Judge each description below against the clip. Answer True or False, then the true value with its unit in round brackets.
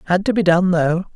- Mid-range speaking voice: True (180 Hz)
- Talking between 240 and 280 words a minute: True (260 wpm)